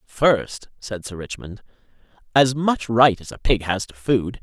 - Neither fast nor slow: Yes, average, 175 wpm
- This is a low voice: Yes, low, 115 Hz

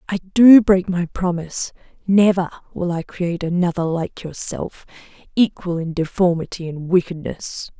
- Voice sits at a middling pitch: Yes, medium, 180 Hz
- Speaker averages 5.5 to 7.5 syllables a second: No, 4.7 syllables/s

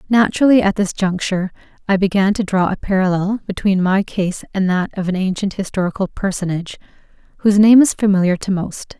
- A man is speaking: No, female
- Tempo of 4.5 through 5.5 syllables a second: No, 5.9 syllables/s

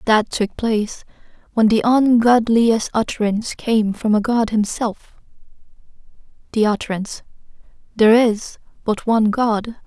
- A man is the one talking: No, female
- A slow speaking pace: Yes, slow, 110 wpm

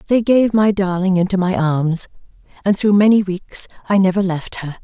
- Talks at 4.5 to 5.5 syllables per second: Yes, 5.0 syllables/s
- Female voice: Yes, female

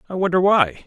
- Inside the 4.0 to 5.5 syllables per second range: No, 5.8 syllables/s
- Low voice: No, medium, 175 Hz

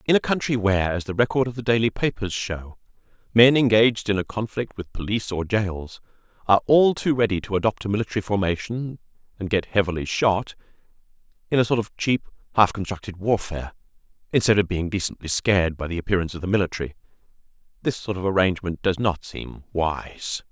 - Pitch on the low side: Yes, low, 100 Hz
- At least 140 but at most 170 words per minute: No, average, 180 wpm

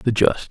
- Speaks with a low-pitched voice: Yes, low, 115 Hz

